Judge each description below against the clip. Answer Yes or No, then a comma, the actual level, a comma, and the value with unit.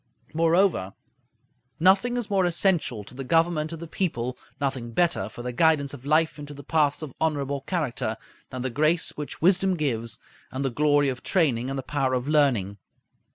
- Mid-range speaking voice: Yes, medium, 145 Hz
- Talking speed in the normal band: Yes, average, 180 wpm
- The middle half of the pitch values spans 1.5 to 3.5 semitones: No, average, 4.3 semitones